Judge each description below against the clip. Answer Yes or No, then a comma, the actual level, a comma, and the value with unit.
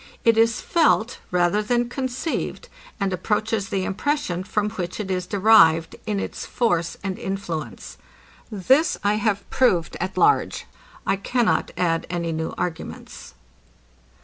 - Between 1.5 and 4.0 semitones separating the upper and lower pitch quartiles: No, average, 4.4 semitones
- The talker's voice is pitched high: Yes, high, 195 Hz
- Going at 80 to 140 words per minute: Yes, slow, 135 wpm